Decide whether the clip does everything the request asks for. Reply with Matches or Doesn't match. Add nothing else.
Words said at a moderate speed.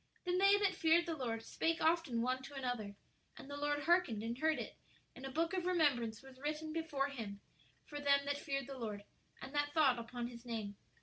Doesn't match